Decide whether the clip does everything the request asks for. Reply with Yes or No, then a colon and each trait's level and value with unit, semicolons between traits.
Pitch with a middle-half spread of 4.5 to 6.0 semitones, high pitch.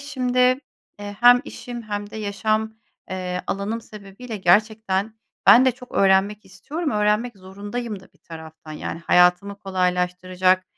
No: average, 3.0 semitones; high, 205 Hz